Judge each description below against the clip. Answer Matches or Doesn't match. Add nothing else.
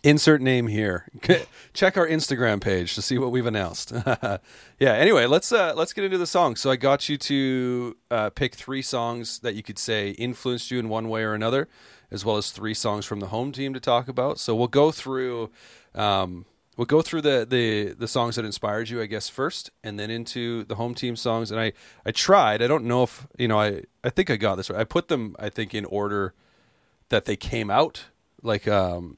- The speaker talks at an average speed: Doesn't match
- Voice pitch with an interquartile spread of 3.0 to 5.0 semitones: Matches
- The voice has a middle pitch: Doesn't match